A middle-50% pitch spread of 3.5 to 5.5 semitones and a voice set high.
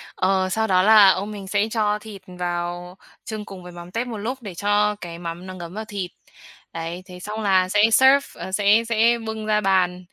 No: average, 3.1 semitones; high, 200 Hz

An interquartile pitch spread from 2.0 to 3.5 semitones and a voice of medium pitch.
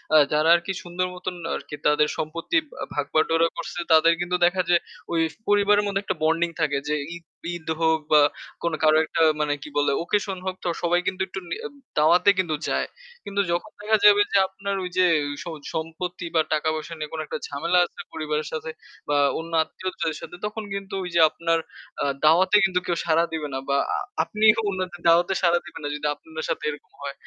Yes: average, 2.9 semitones; medium, 170 Hz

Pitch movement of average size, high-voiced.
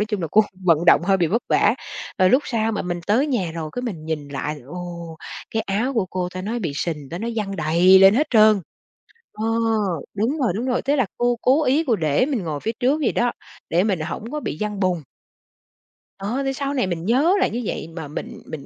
No: wide, 6.1 semitones; high, 200 Hz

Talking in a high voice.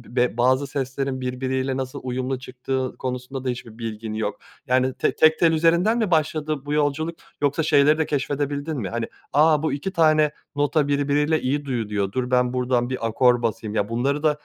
No: low, 135 Hz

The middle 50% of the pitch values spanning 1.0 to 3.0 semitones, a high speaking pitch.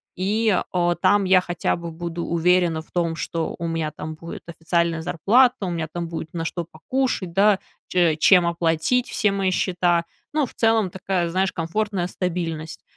No: narrow, 2.5 semitones; medium, 175 Hz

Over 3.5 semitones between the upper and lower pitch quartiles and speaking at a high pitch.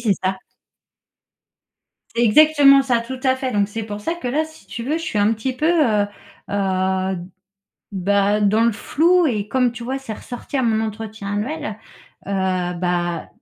Yes: average, 4.7 semitones; high, 220 Hz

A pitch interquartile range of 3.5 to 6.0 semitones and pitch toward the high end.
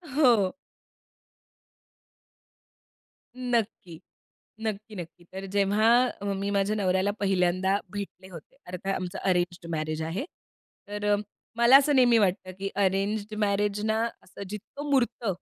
No: average, 3.0 semitones; high, 200 Hz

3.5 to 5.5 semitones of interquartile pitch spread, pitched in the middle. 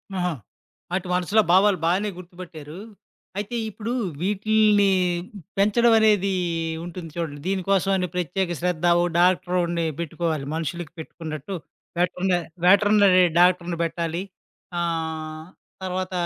No: narrow, 2.6 semitones; medium, 180 Hz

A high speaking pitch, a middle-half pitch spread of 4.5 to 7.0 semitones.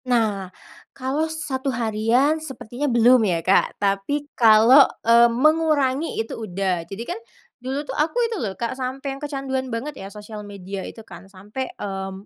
Yes: high, 235 Hz; average, 5.1 semitones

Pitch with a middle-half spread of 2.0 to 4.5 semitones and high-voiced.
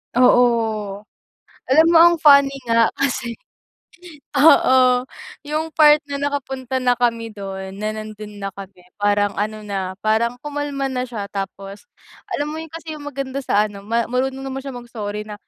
No: average, 4.9 semitones; high, 245 Hz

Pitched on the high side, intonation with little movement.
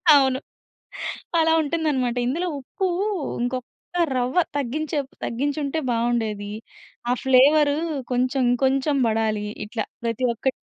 No: very high, 260 Hz; average, 3.2 semitones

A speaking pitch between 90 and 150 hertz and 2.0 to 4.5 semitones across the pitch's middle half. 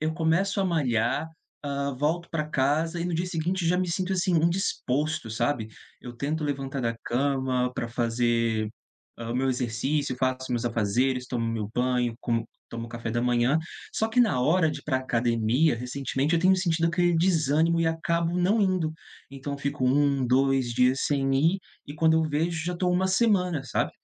No: medium, 140 Hz; average, 5.2 semitones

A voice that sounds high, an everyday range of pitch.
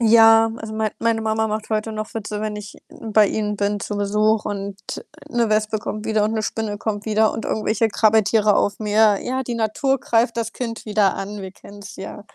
No: high, 215 Hz; narrow, 1.2 semitones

